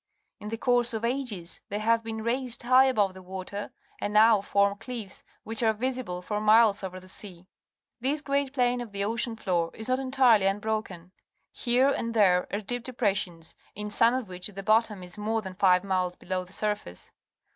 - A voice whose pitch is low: No, high, 215 Hz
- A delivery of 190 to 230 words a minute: Yes, average, 200 wpm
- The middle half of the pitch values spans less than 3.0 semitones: No, average, 3.8 semitones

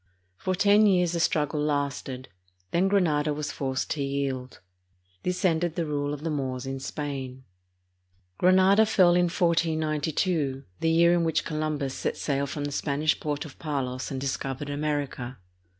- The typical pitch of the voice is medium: Yes, medium, 150 Hz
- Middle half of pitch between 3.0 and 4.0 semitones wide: Yes, average, 3.5 semitones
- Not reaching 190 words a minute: Yes, average, 155 wpm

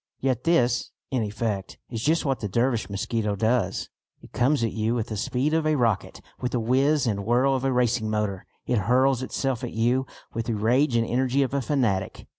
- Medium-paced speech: No, fast, 210 wpm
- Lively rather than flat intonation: No, average, 3.3 semitones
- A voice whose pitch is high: No, low, 120 Hz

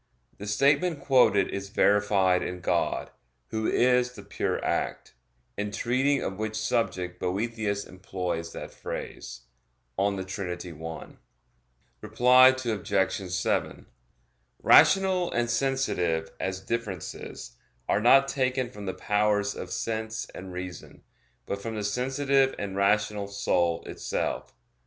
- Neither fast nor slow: No, slow, 120 wpm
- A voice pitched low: Yes, low, 105 Hz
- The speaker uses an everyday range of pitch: Yes, average, 4.7 semitones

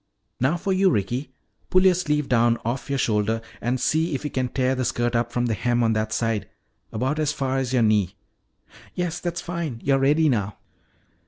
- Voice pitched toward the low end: Yes, low, 130 Hz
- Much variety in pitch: No, average, 4.5 semitones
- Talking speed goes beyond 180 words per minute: Yes, average, 200 wpm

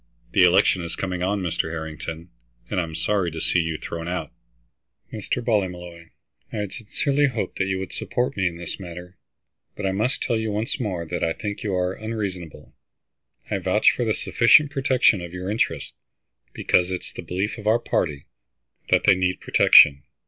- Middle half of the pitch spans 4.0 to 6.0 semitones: No, average, 3.5 semitones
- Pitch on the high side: No, very low, 95 Hz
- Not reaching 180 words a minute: No, average, 190 wpm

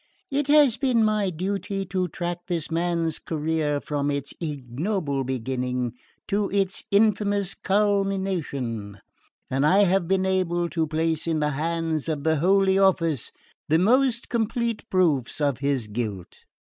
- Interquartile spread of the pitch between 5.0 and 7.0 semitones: Yes, average, 5.3 semitones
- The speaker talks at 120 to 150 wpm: Yes, average, 140 wpm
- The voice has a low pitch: No, medium, 170 Hz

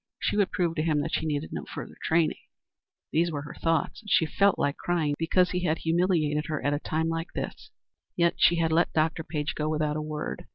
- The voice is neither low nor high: Yes, medium, 160 Hz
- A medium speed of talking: No, fast, 230 wpm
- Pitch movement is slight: Yes, narrow, 2.0 semitones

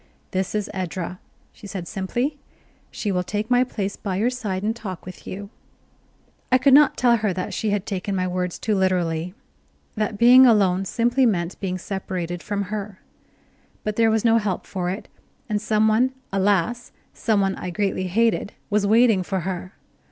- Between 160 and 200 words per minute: Yes, average, 180 wpm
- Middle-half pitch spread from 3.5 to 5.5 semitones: No, average, 3.1 semitones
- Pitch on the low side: No, high, 200 Hz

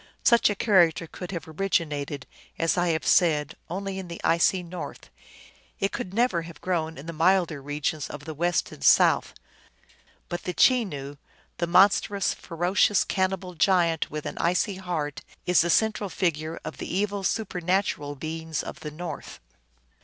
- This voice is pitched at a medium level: Yes, medium, 175 Hz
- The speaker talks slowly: No, average, 160 wpm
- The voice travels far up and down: No, average, 3.2 semitones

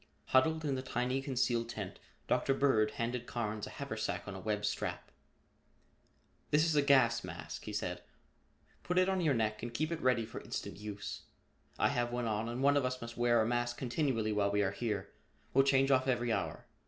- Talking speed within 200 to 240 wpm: Yes, fast, 205 wpm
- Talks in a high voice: No, low, 120 Hz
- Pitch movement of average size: Yes, average, 3.7 semitones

